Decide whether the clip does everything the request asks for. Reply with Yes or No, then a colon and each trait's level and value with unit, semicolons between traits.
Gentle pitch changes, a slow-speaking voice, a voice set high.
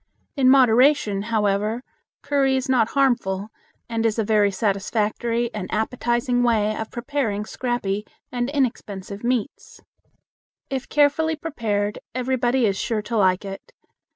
No: average, 3.7 semitones; slow, 125 wpm; high, 230 Hz